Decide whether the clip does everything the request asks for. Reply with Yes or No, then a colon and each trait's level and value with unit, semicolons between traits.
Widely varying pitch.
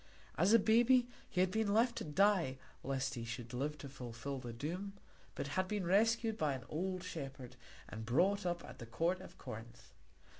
Yes: wide, 7.4 semitones